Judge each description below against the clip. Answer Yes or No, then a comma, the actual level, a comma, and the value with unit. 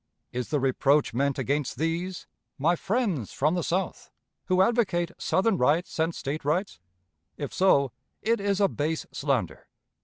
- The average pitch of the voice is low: No, medium, 160 Hz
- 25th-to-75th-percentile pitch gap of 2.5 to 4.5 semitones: No, average, 5.2 semitones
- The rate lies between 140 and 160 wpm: Yes, average, 150 wpm